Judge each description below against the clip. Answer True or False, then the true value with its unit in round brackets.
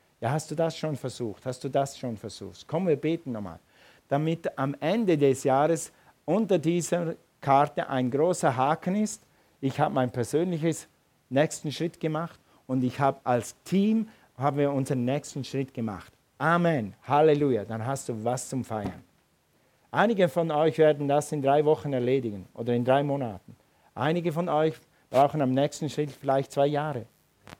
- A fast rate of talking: False (165 wpm)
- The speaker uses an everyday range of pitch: True (3.6 semitones)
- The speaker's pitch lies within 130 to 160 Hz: True (140 Hz)